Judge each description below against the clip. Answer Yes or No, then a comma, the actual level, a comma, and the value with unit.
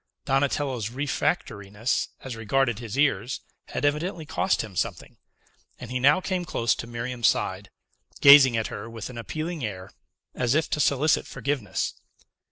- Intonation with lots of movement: No, average, 4.2 semitones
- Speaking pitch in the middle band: No, low, 130 Hz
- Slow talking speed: No, average, 150 wpm